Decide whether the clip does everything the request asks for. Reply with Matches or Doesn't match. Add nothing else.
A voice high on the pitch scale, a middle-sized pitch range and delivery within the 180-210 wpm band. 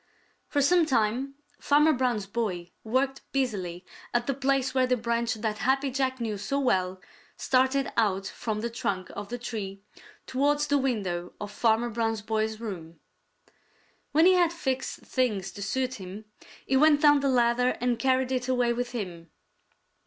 Doesn't match